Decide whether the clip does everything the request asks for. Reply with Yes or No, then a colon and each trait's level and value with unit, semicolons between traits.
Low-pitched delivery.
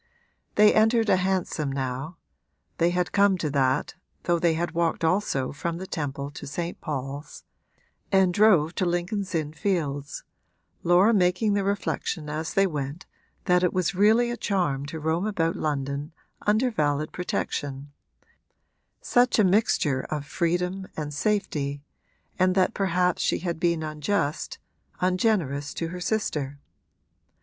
No: medium, 170 Hz